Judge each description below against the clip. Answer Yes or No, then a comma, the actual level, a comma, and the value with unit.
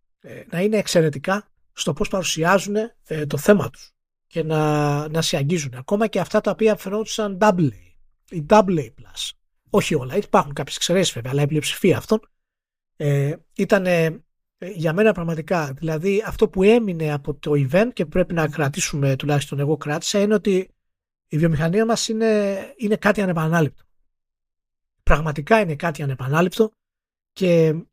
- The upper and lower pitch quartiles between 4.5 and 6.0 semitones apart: Yes, wide, 5.4 semitones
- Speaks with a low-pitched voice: No, medium, 170 Hz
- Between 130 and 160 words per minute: Yes, average, 145 wpm